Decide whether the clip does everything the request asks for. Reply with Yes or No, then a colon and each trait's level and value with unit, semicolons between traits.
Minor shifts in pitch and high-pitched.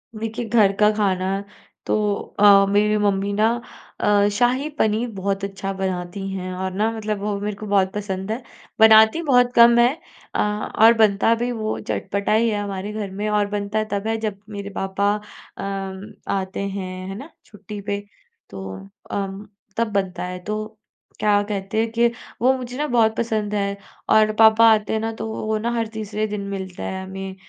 Yes: narrow, 2.1 semitones; high, 210 Hz